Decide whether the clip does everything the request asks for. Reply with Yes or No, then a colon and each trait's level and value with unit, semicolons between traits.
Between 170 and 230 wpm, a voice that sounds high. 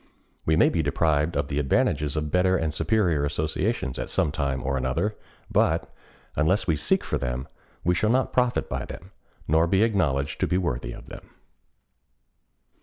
No: average, 175 wpm; very low, 80 Hz